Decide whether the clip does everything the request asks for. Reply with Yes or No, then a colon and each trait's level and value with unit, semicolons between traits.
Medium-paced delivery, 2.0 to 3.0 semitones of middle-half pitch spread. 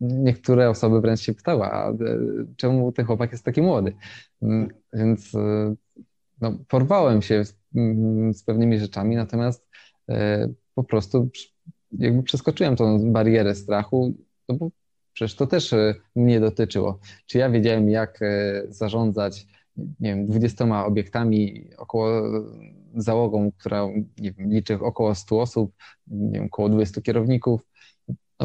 Yes: average, 120 wpm; narrow, 2.4 semitones